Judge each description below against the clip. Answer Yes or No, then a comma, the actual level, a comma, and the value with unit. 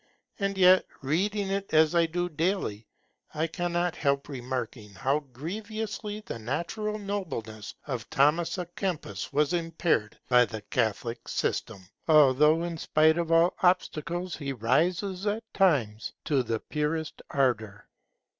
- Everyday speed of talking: No, slow, 130 wpm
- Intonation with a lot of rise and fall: Yes, wide, 5.9 semitones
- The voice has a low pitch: No, medium, 160 Hz